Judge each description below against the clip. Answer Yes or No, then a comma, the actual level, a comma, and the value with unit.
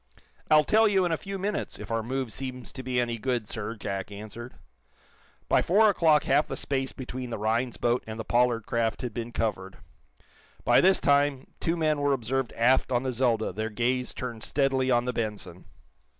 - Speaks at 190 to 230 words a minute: Yes, average, 195 wpm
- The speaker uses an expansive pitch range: No, average, 3.2 semitones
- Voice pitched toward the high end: No, low, 125 Hz